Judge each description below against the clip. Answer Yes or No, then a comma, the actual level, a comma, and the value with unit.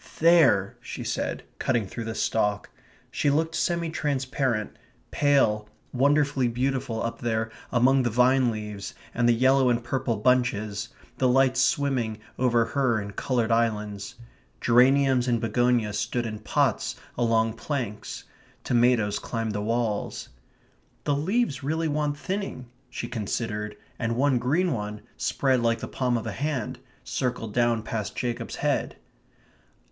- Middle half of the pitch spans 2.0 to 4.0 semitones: Yes, average, 3.3 semitones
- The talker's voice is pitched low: Yes, low, 120 Hz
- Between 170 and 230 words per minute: No, average, 140 wpm